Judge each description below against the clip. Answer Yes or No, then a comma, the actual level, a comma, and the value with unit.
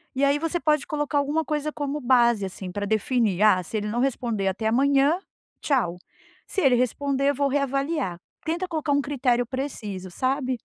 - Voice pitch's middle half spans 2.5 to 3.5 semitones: No, average, 4.7 semitones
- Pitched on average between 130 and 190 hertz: No, very high, 270 Hz